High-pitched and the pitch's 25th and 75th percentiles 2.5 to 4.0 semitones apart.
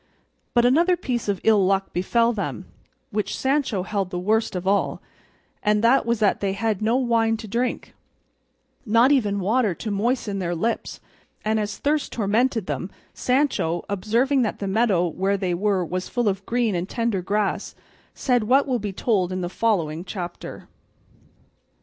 Yes: high, 210 Hz; average, 3.7 semitones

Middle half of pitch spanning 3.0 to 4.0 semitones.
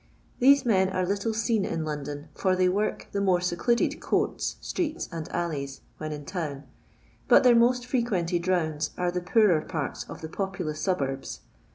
No: average, 5.2 semitones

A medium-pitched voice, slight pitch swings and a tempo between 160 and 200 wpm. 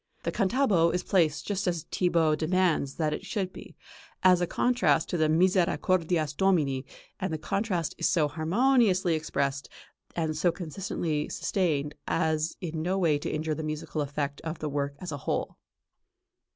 No: medium, 165 Hz; average, 3.3 semitones; average, 165 wpm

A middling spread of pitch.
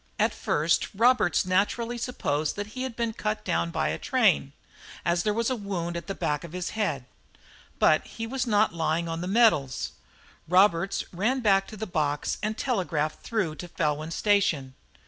Yes: average, 5.0 semitones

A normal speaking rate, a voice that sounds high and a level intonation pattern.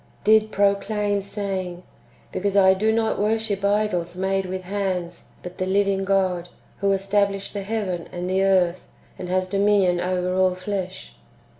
Yes: average, 160 wpm; high, 195 Hz; narrow, 1.7 semitones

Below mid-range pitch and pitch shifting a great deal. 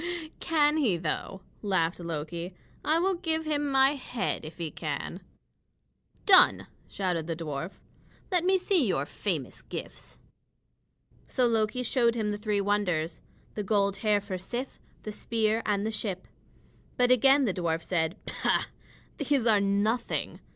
No: high, 210 Hz; wide, 6.7 semitones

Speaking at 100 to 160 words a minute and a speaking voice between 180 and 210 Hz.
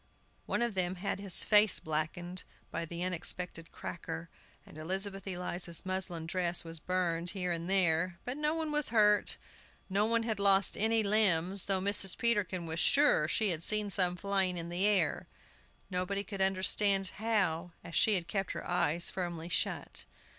No: average, 170 wpm; medium, 185 Hz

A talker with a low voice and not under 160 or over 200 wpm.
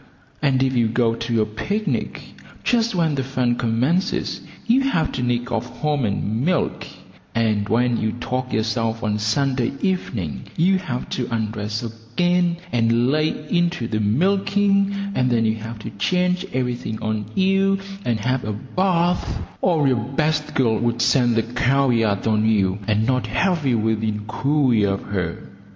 Yes: low, 120 Hz; average, 165 wpm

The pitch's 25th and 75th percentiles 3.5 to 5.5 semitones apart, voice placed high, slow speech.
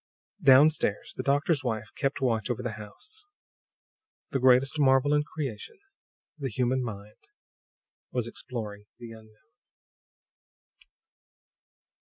No: average, 4.0 semitones; low, 130 Hz; slow, 110 wpm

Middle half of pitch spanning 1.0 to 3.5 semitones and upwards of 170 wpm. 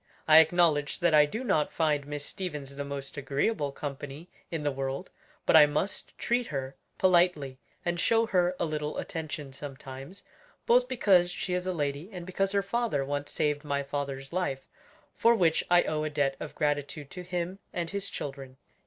No: average, 4.1 semitones; average, 180 wpm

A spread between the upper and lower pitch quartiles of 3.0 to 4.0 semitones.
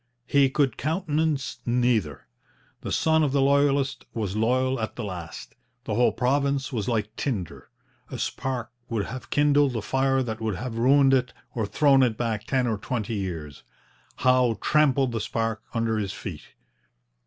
Yes: average, 3.7 semitones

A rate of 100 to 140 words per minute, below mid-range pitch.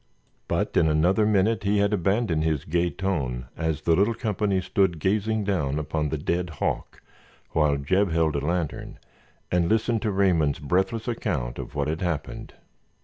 No: average, 165 wpm; very low, 90 Hz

